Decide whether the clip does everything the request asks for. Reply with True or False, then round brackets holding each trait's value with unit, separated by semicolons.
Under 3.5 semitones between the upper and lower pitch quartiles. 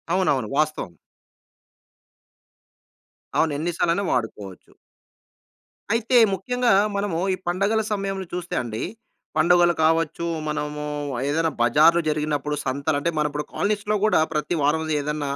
False (4.3 semitones)